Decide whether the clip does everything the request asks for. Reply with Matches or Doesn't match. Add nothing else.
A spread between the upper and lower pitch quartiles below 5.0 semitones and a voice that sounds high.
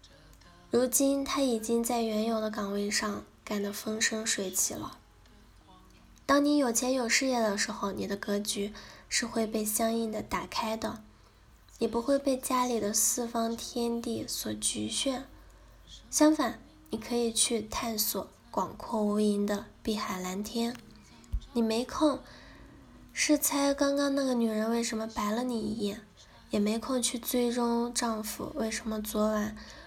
Matches